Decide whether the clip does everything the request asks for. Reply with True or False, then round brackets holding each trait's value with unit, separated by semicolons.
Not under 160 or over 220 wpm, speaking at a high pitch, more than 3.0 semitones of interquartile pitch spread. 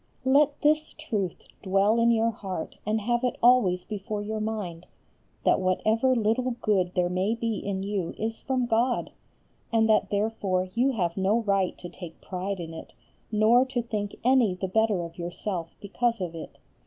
True (175 wpm; 215 Hz; 4.0 semitones)